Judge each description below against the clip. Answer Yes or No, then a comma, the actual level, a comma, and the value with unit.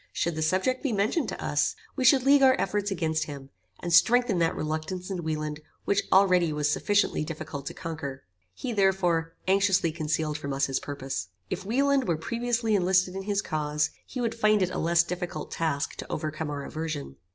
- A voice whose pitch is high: No, medium, 175 Hz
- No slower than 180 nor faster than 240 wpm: Yes, average, 190 wpm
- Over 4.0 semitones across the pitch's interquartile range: Yes, average, 4.8 semitones